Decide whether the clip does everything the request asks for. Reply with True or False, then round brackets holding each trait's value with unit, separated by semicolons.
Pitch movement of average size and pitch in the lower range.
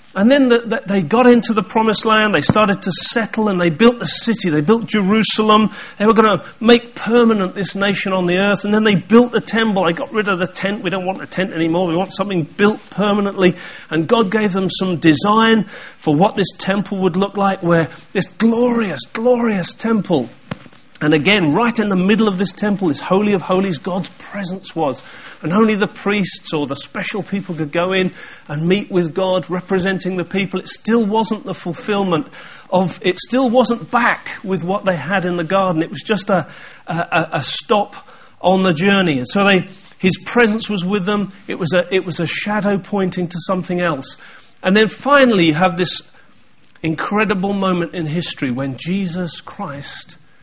False (3.1 semitones; 195 Hz)